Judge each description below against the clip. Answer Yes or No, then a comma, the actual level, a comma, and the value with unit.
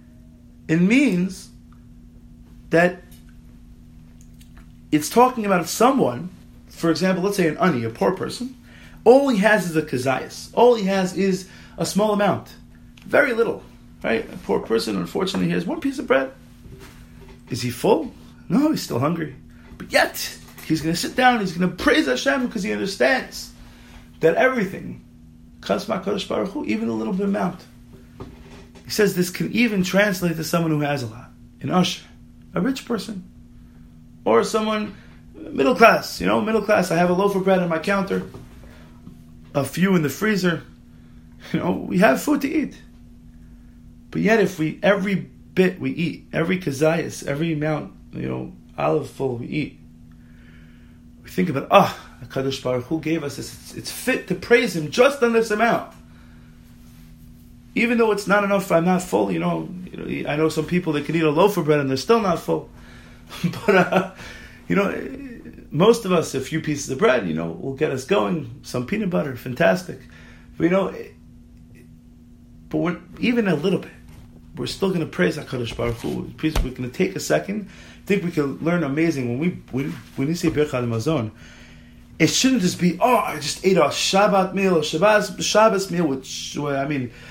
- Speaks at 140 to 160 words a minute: No, average, 180 wpm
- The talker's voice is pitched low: No, medium, 160 Hz